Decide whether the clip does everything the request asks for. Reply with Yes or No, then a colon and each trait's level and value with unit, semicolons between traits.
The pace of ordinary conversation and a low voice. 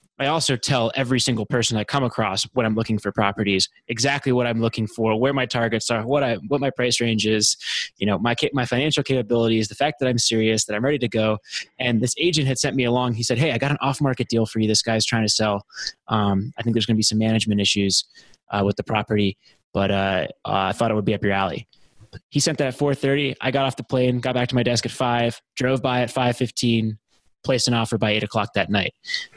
No: fast, 245 wpm; low, 120 Hz